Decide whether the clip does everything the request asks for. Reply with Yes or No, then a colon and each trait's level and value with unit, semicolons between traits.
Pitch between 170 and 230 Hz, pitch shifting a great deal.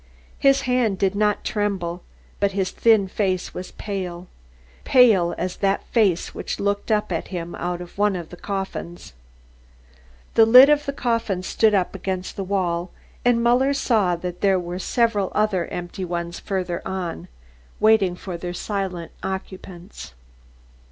No: high, 190 Hz; average, 3.2 semitones